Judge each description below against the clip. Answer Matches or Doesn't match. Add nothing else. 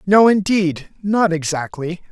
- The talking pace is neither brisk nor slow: Doesn't match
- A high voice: Doesn't match